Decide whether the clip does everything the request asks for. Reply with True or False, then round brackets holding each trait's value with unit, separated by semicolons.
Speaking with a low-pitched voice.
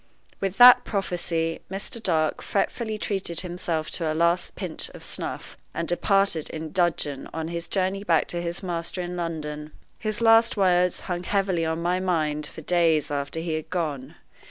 False (175 Hz)